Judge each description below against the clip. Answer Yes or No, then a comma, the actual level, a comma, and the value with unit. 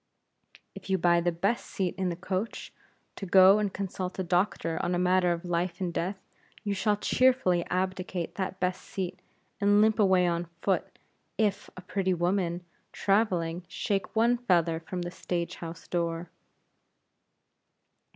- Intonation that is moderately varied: No, narrow, 2.2 semitones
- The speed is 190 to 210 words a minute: No, average, 155 wpm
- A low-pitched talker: No, medium, 185 Hz